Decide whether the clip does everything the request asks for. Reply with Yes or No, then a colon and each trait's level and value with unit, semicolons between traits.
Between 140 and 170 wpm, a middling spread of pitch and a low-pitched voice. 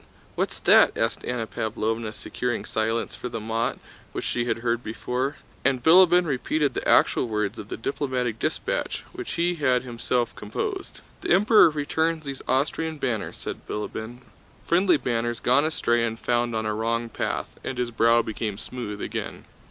Yes: average, 165 wpm; average, 4.0 semitones; low, 120 Hz